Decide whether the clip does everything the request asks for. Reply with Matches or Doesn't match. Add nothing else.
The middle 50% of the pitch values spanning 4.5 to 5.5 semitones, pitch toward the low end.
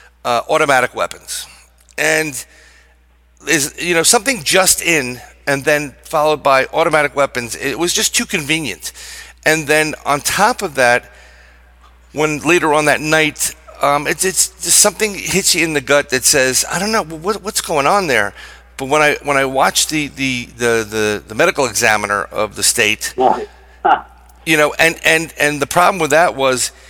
Doesn't match